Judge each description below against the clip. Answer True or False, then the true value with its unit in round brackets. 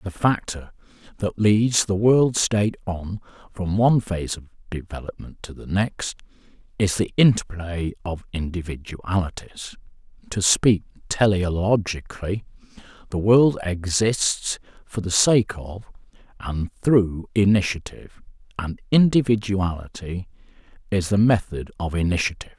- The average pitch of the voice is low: True (95 Hz)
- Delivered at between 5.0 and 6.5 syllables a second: False (4.4 syllables/s)